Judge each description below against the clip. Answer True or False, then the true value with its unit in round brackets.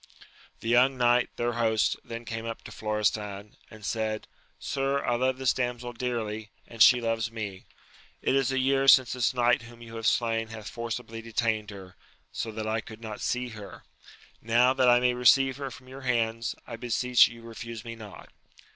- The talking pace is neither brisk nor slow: True (190 wpm)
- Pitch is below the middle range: True (115 Hz)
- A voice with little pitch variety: True (1.9 semitones)